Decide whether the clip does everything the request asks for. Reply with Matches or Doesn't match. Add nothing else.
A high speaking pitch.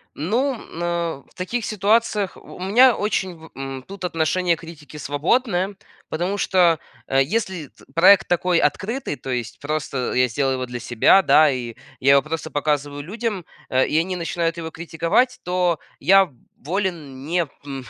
Doesn't match